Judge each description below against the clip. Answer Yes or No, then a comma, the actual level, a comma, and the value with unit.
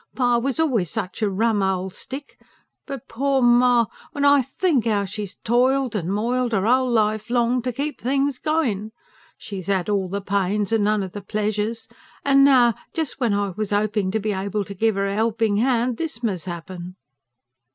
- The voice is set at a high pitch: Yes, high, 220 Hz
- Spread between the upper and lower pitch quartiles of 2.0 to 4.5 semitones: Yes, average, 3.9 semitones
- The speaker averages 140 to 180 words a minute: No, average, 190 wpm